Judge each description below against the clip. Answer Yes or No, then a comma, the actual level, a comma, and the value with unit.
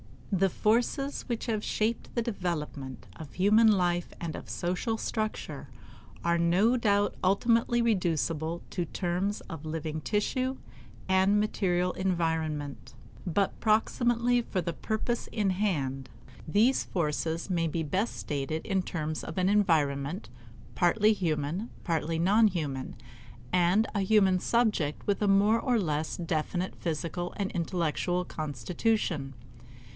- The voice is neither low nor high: Yes, medium, 180 Hz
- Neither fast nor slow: No, slow, 130 wpm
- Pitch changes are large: No, average, 4.8 semitones